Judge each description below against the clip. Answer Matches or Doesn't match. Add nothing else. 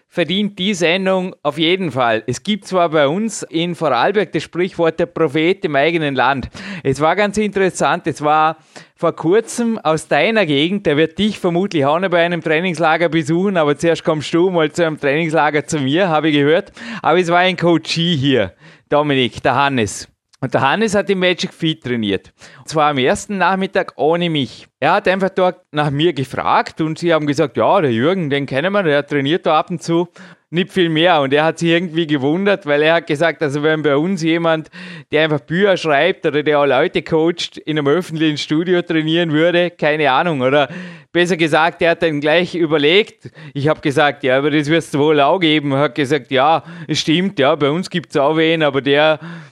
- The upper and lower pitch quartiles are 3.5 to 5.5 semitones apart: Doesn't match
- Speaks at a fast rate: Matches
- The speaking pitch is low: Doesn't match